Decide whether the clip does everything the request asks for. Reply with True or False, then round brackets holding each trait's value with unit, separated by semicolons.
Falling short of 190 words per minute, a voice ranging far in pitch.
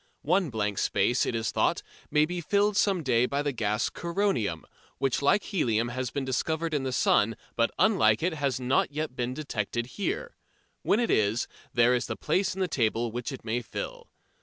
False (195 wpm; 6.2 semitones)